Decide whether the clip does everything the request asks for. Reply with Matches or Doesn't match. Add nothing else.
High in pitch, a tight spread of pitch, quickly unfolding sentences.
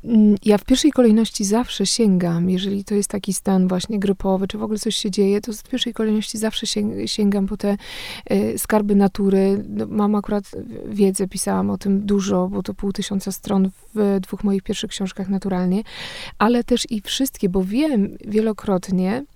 Matches